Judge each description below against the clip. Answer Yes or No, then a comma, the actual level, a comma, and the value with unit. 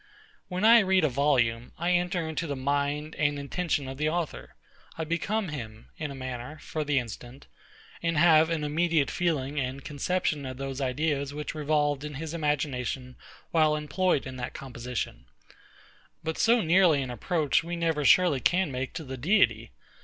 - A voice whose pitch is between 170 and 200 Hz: No, medium, 150 Hz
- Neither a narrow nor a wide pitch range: Yes, average, 3.8 semitones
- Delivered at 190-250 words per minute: No, average, 170 wpm